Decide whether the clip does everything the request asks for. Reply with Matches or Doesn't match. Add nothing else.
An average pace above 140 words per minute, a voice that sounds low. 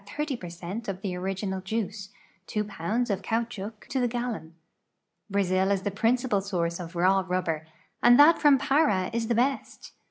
Doesn't match